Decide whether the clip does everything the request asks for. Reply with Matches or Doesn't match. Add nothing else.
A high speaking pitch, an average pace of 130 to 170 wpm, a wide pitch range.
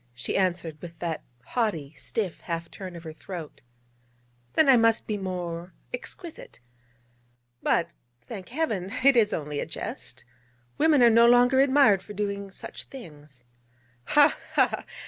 Matches